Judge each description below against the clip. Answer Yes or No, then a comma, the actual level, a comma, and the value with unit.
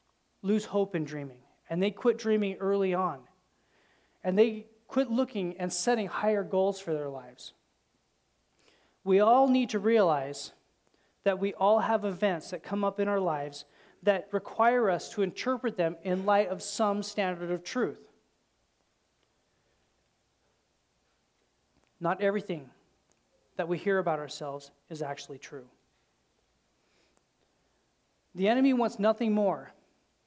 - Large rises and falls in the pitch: No, average, 3.9 semitones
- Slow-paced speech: Yes, slow, 130 wpm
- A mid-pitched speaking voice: No, high, 195 Hz